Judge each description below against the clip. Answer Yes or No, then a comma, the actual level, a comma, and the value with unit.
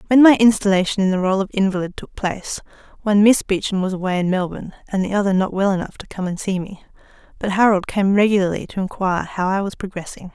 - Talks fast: Yes, fast, 220 wpm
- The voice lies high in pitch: Yes, high, 195 Hz